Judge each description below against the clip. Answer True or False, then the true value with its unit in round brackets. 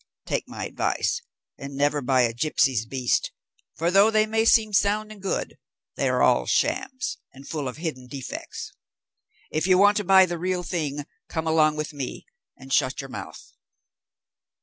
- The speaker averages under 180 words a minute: True (170 wpm)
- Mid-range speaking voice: True (160 Hz)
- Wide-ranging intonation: True (6.5 semitones)